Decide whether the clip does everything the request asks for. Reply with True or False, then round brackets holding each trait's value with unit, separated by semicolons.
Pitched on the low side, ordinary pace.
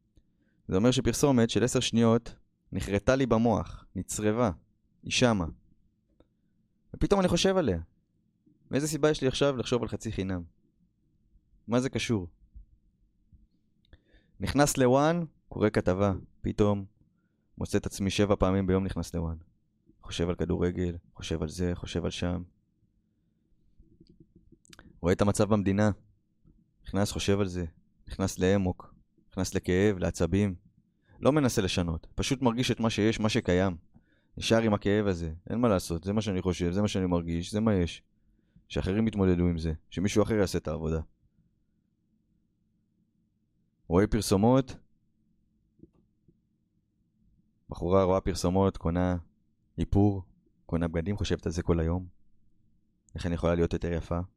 True (100 Hz; 130 wpm)